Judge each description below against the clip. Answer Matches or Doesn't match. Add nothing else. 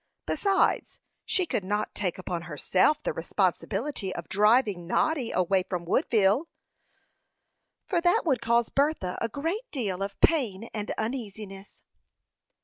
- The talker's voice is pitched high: Matches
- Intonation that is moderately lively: Doesn't match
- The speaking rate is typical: Doesn't match